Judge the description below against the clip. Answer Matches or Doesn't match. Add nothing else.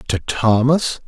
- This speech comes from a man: Matches